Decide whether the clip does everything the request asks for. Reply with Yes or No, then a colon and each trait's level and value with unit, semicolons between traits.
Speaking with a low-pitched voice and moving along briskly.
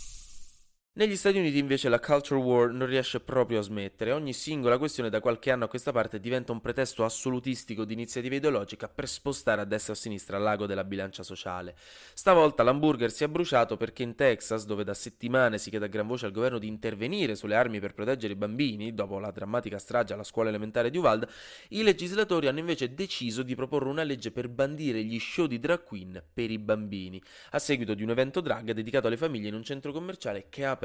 Yes: low, 120 Hz; fast, 210 wpm